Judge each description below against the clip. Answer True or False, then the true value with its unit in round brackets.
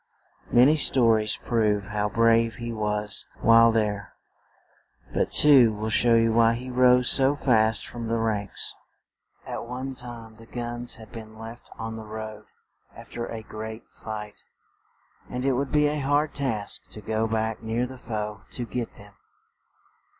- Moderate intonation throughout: False (2.2 semitones)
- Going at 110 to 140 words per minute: False (165 wpm)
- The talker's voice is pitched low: True (115 Hz)